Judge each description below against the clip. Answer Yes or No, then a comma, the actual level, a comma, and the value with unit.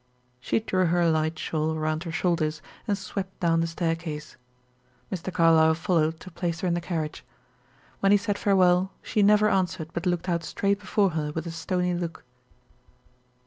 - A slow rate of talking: No, average, 175 wpm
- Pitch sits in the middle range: Yes, medium, 170 Hz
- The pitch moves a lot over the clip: No, average, 2.7 semitones